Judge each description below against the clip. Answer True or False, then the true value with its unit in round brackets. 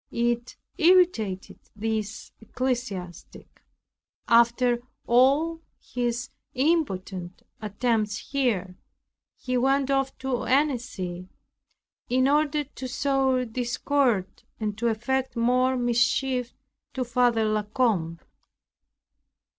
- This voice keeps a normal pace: False (90 wpm)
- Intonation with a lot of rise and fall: False (3.4 semitones)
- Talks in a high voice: True (245 Hz)